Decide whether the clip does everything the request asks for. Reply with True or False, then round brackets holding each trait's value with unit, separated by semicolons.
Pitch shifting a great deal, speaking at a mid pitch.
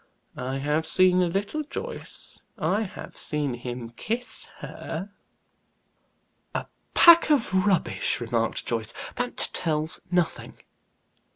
True (8.0 semitones; 170 Hz)